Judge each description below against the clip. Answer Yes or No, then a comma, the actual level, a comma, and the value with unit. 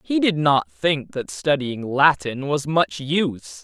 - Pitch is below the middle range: No, medium, 145 Hz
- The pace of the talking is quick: No, average, 165 wpm